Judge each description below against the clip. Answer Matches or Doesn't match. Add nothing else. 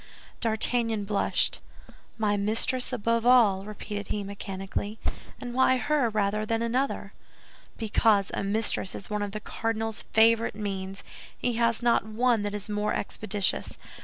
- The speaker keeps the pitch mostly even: Matches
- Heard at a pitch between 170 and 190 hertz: Doesn't match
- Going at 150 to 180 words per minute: Doesn't match